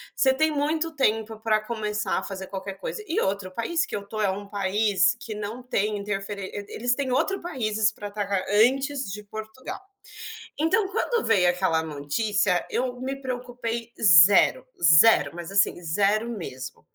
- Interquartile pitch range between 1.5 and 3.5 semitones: No, average, 4.2 semitones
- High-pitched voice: Yes, high, 215 Hz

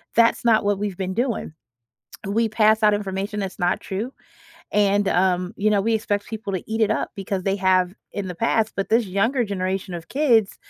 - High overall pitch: Yes, high, 205 Hz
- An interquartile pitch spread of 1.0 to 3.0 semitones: Yes, narrow, 2.5 semitones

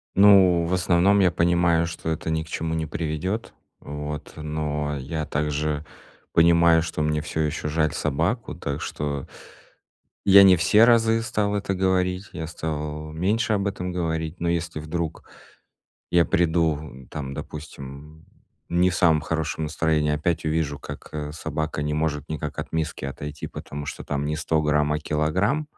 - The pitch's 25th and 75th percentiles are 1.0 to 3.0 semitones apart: Yes, narrow, 2.6 semitones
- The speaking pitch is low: Yes, very low, 80 Hz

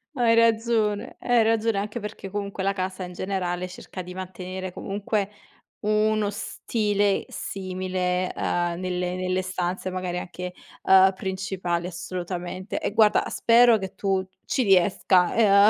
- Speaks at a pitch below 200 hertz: Yes, high, 190 Hz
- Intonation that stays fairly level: Yes, narrow, 2.3 semitones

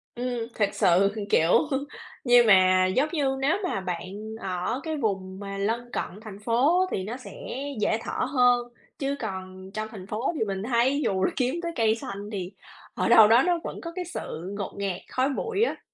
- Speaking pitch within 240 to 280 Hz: No, high, 220 Hz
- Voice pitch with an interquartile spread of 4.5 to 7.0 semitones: Yes, average, 5.2 semitones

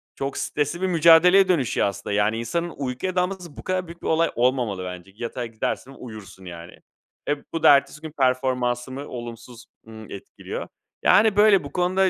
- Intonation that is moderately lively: No, wide, 6.9 semitones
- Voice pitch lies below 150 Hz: Yes, low, 135 Hz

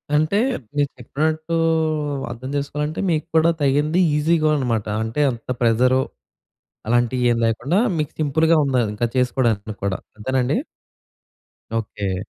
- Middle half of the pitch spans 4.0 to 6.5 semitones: Yes, average, 4.7 semitones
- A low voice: Yes, low, 130 Hz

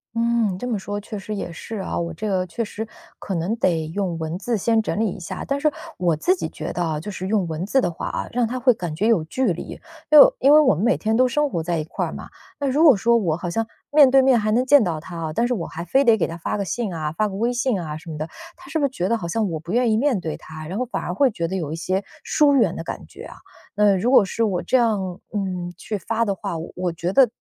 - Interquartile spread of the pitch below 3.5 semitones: No, wide, 5.6 semitones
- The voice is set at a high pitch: Yes, high, 205 Hz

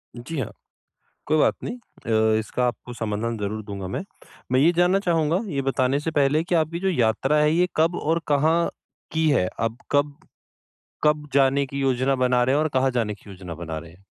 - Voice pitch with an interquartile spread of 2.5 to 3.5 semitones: No, average, 5.3 semitones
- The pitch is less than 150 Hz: Yes, low, 135 Hz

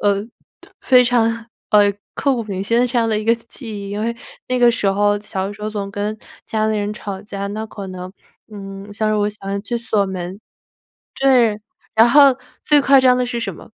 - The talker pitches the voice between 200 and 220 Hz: Yes, high, 215 Hz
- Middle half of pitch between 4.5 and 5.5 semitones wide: No, average, 2.7 semitones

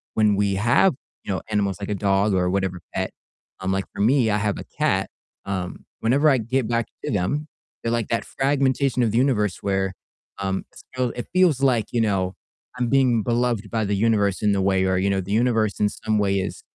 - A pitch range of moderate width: Yes, average, 3.7 semitones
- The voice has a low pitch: Yes, low, 105 Hz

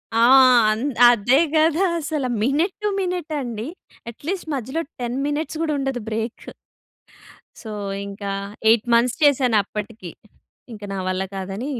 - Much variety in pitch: Yes, wide, 5.7 semitones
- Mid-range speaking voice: No, high, 245 Hz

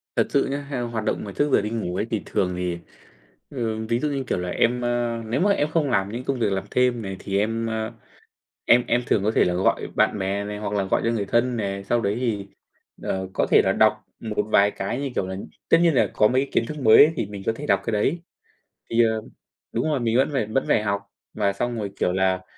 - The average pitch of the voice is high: No, low, 110 Hz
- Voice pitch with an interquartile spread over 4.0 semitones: No, average, 3.5 semitones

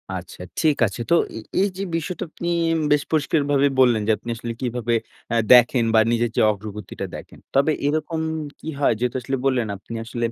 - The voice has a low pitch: Yes, low, 125 Hz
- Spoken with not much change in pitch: No, average, 4.2 semitones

